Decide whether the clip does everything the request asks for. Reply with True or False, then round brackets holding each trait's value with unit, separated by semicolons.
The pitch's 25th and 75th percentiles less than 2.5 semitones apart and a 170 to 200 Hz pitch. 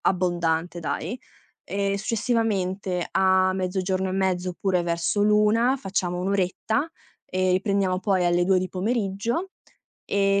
True (1.8 semitones; 190 Hz)